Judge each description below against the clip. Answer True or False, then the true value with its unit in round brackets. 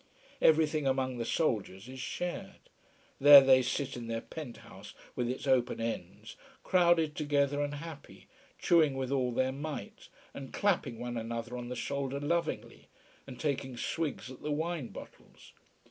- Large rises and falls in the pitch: False (3.5 semitones)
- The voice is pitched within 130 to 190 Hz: True (135 Hz)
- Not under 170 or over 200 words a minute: False (155 wpm)